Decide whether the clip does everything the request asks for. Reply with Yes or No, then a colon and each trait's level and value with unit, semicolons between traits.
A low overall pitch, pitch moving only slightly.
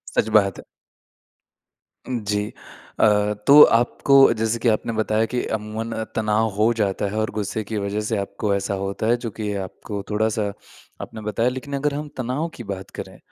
Yes: low, 110 Hz; narrow, 2.1 semitones